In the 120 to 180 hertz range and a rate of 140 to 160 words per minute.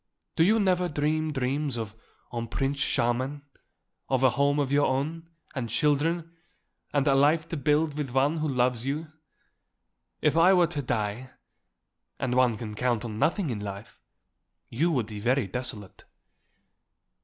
Yes: low, 135 Hz; average, 155 wpm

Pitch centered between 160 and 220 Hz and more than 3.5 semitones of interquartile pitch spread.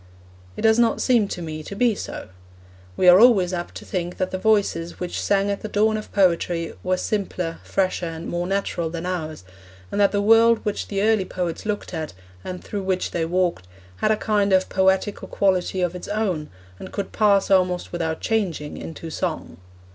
No: medium, 185 Hz; average, 3.0 semitones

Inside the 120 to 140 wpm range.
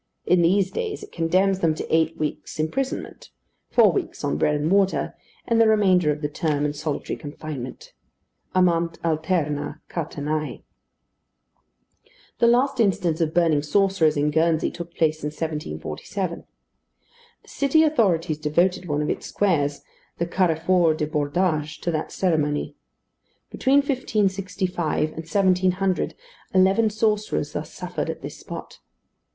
Yes: slow, 135 wpm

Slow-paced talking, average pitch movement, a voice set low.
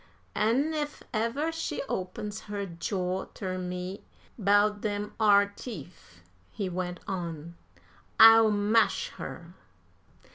No: slow, 110 wpm; average, 3.4 semitones; high, 205 Hz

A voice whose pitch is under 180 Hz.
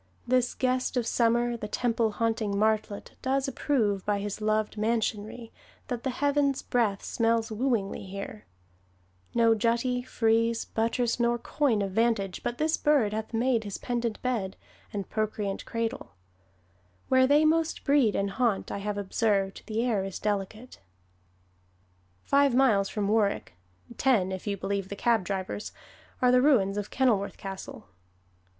No: high, 225 Hz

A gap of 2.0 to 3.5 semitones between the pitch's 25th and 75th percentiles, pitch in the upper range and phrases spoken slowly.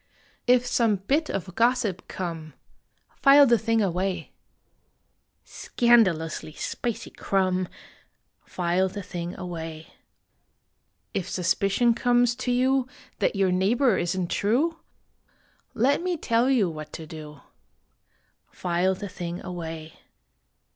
No: wide, 5.6 semitones; high, 195 Hz; slow, 115 wpm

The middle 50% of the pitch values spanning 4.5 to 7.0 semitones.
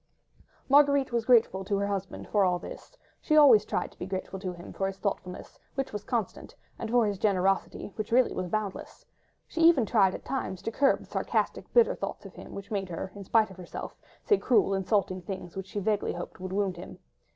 No: average, 3.7 semitones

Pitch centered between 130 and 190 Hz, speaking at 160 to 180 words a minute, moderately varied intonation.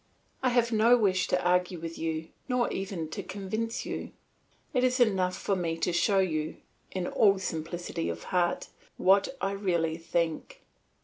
Yes: medium, 185 Hz; average, 165 wpm; average, 4.3 semitones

